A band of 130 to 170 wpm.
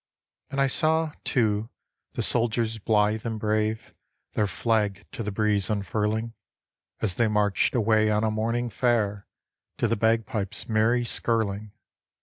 Yes: slow, 135 wpm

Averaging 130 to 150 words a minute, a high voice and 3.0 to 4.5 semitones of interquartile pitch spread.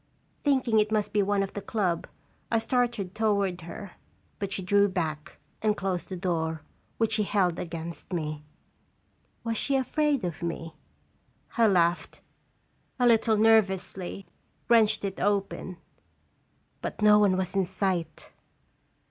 Yes: average, 140 wpm; high, 195 Hz; average, 3.5 semitones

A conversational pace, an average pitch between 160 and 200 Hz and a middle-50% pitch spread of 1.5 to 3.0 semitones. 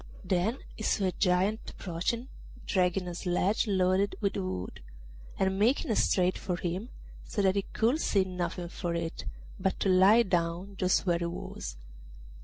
Yes: average, 160 wpm; medium, 185 Hz; narrow, 2.4 semitones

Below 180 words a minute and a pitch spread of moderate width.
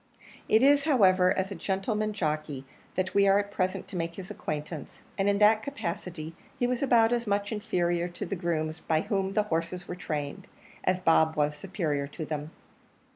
No: average, 185 wpm; average, 4.2 semitones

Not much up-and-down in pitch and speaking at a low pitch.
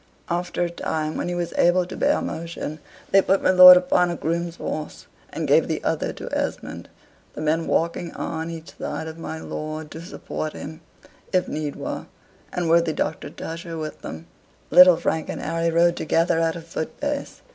No: narrow, 1.7 semitones; medium, 165 Hz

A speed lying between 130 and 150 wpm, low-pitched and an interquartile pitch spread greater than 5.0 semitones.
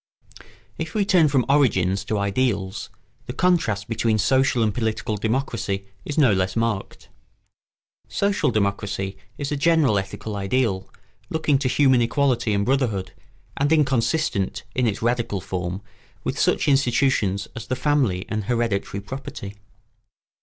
Yes: average, 140 wpm; low, 115 Hz; wide, 5.4 semitones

